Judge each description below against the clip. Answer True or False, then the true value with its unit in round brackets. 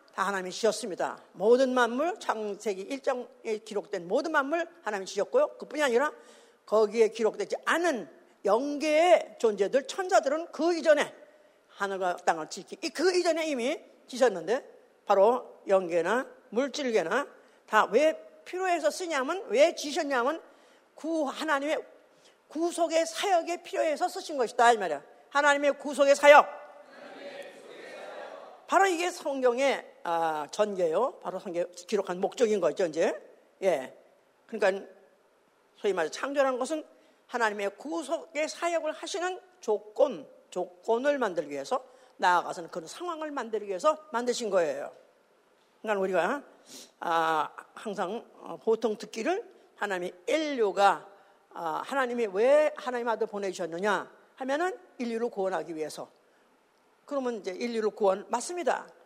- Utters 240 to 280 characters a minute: False (295 characters per minute)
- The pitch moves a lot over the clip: True (7.6 semitones)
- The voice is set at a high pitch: True (270 Hz)